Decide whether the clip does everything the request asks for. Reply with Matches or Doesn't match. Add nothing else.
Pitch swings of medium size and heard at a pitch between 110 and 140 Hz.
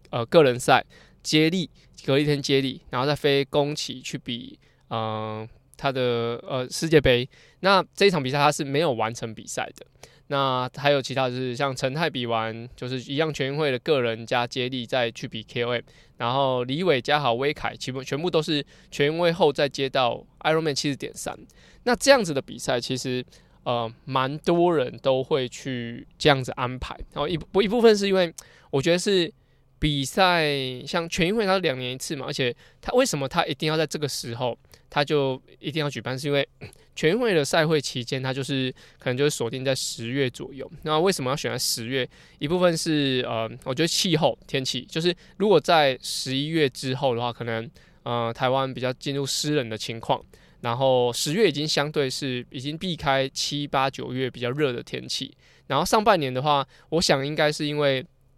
Matches